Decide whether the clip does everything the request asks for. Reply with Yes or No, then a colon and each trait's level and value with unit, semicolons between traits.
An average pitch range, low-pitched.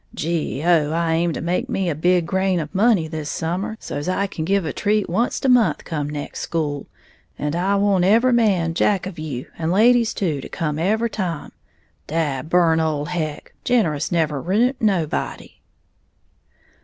No: average, 4.1 semitones; medium, 170 Hz